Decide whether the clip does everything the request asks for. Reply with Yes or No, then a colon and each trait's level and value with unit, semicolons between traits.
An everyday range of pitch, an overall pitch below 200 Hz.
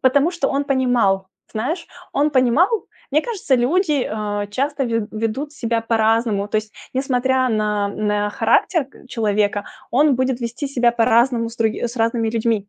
No: average, 3.9 semitones; high, 235 Hz